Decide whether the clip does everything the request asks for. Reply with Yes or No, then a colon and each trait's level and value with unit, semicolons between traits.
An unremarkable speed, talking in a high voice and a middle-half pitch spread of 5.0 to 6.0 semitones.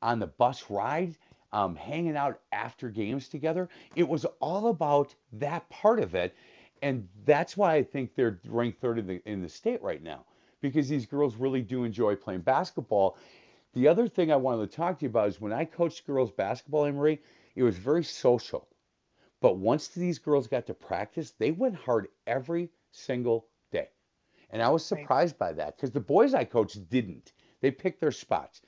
No: average, 190 wpm; medium, 140 Hz; average, 5.3 semitones